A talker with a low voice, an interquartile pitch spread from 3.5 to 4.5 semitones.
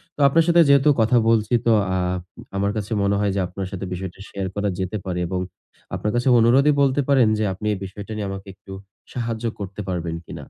Yes: low, 105 Hz; average, 4.0 semitones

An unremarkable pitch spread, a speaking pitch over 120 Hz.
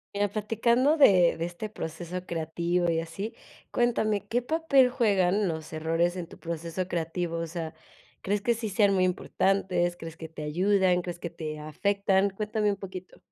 Yes: average, 3.7 semitones; medium, 185 Hz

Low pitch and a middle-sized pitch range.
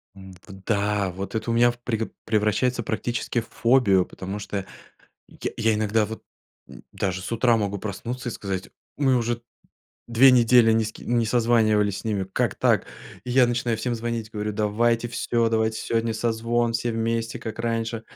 No: low, 115 Hz; narrow, 2.2 semitones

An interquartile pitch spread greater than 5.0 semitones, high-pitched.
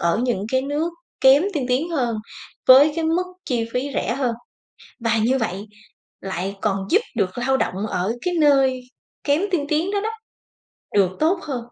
Yes: wide, 5.4 semitones; very high, 260 Hz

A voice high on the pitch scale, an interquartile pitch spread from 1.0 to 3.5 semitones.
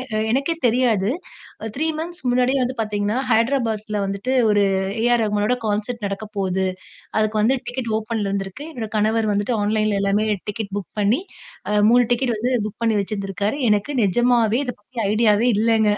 Yes: high, 220 Hz; average, 3.0 semitones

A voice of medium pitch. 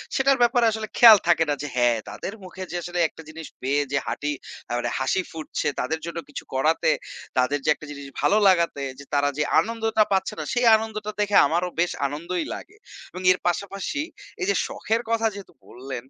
Yes: medium, 175 Hz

